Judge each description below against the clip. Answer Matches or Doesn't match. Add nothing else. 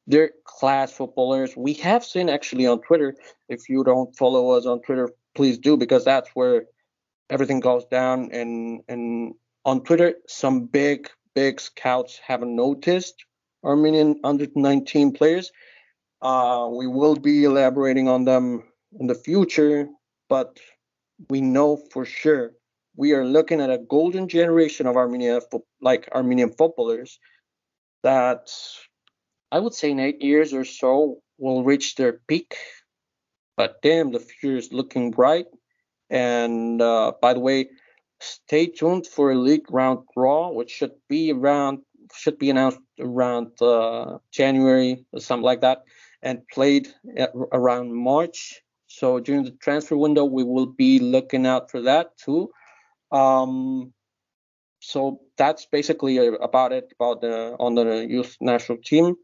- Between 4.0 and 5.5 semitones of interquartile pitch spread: Doesn't match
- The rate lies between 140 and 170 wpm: Matches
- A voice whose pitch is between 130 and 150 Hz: Matches